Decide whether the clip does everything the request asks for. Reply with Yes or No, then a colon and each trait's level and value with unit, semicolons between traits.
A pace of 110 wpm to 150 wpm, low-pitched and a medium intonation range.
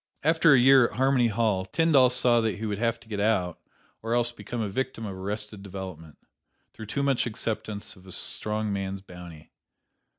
No: average, 190 wpm; low, 110 Hz; average, 3.8 semitones